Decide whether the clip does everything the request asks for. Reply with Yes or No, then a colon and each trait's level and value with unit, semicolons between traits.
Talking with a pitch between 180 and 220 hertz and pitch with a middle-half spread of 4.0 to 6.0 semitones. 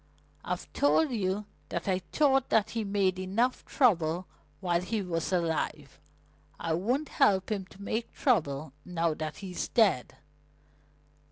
Yes: high, 190 Hz; average, 4.6 semitones